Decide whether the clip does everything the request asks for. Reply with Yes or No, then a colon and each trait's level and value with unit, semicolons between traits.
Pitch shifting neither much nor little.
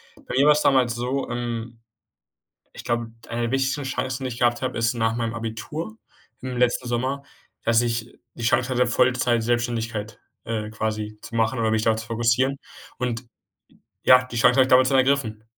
No: narrow, 2.1 semitones